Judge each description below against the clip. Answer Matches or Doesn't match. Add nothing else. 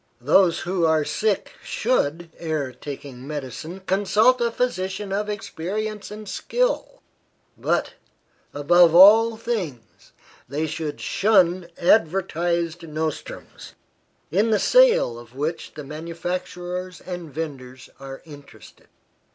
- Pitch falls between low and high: Matches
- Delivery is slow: Matches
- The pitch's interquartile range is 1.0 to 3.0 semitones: Doesn't match